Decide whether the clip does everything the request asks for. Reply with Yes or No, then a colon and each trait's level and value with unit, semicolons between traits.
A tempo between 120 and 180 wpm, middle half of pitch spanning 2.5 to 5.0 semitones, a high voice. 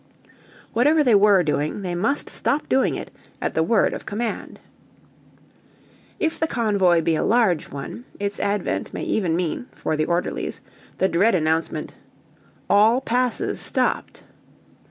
No: average, 140 wpm; wide, 5.6 semitones; high, 200 Hz